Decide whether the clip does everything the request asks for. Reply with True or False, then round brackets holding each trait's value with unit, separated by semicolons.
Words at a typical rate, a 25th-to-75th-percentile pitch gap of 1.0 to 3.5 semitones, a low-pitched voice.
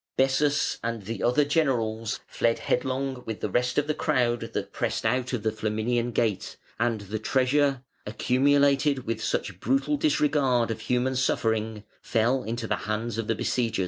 True (165 wpm; 3.2 semitones; 120 Hz)